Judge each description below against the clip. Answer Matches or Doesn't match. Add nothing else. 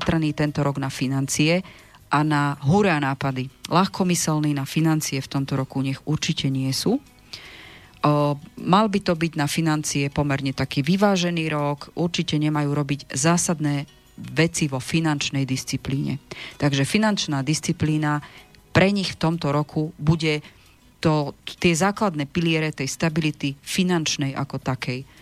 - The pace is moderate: Matches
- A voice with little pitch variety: Doesn't match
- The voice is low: Doesn't match